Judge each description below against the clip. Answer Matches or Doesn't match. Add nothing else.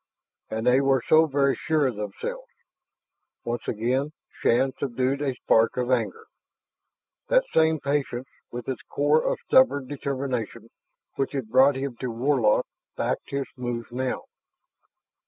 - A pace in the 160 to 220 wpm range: Doesn't match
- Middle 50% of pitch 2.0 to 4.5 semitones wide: Matches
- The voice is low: Matches